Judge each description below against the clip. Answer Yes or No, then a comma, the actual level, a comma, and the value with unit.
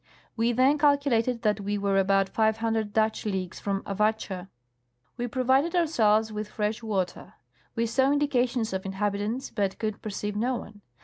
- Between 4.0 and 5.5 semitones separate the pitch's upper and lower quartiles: No, average, 3.2 semitones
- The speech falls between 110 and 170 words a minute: Yes, average, 165 wpm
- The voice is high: Yes, high, 220 Hz